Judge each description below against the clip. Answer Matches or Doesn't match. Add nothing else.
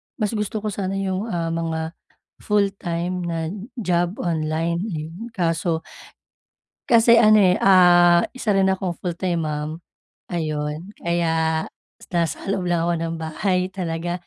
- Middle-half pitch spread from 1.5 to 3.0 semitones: Matches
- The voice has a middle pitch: Matches